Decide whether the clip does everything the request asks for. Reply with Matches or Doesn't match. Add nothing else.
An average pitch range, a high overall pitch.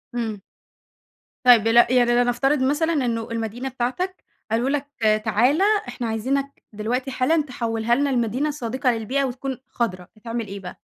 Matches